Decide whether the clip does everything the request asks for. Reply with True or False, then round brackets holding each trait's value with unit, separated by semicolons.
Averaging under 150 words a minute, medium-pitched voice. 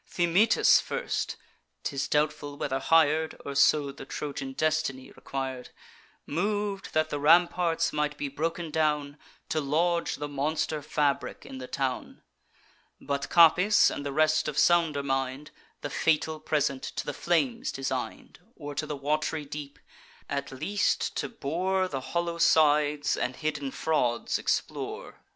True (140 wpm; 150 Hz)